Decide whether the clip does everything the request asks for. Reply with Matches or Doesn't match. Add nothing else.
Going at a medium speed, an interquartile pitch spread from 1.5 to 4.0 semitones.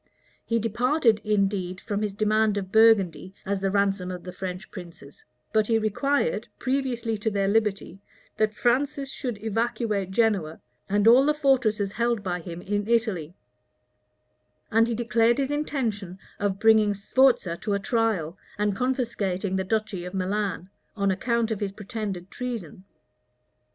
Matches